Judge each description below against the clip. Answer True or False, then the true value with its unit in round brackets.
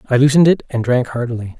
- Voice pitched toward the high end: False (130 Hz)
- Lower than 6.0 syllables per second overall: False (7.1 syllables/s)